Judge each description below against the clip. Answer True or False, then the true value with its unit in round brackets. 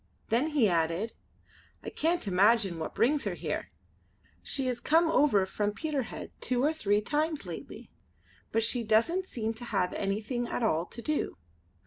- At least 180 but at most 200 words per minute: False (160 wpm)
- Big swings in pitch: True (6.3 semitones)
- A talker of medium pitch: False (230 Hz)